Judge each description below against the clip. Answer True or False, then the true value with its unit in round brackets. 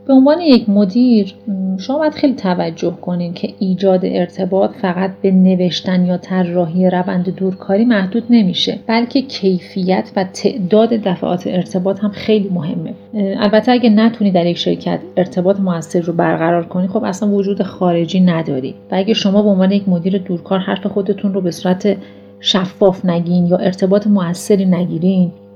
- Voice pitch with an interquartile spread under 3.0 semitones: True (2.5 semitones)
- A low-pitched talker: False (190 Hz)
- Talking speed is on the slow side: False (155 wpm)